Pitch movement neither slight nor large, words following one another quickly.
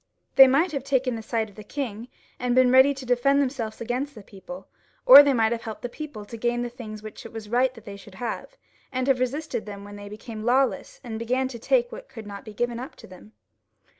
Yes: average, 3.4 semitones; fast, 245 wpm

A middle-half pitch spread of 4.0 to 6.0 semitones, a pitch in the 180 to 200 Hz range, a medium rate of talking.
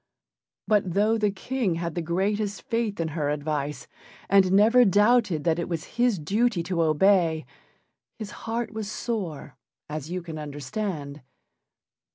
Yes: average, 5.2 semitones; medium, 185 Hz; average, 145 wpm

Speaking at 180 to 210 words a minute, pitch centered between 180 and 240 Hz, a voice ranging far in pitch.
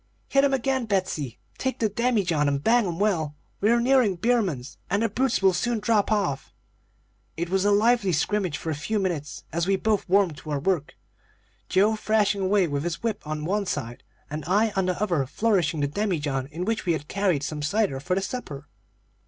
Yes: average, 200 wpm; high, 190 Hz; wide, 5.8 semitones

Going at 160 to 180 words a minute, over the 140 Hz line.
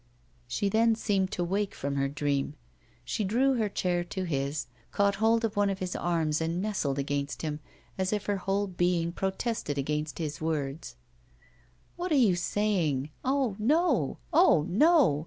Yes: average, 165 wpm; medium, 185 Hz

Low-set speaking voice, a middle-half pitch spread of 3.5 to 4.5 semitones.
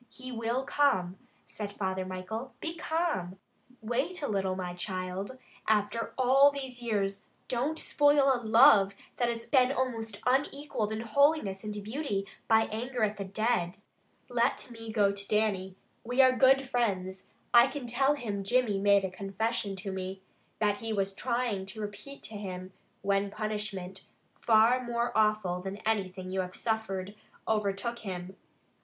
No: high, 215 Hz; average, 4.1 semitones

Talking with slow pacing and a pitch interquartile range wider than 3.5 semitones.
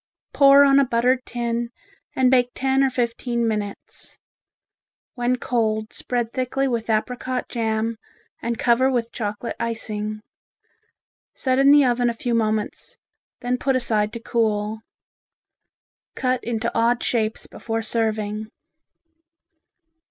No: slow, 120 wpm; narrow, 2.4 semitones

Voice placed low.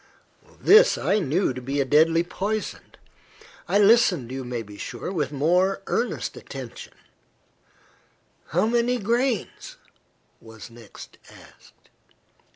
No: medium, 175 Hz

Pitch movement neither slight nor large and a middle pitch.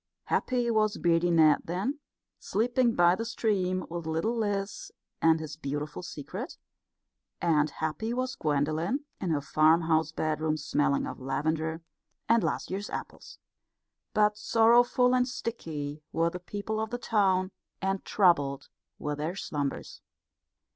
No: wide, 5.8 semitones; medium, 175 Hz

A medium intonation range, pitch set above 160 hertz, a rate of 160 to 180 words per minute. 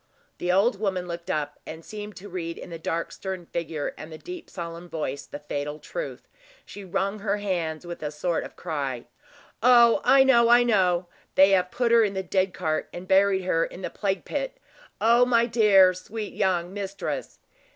No: average, 3.9 semitones; high, 190 Hz; average, 195 wpm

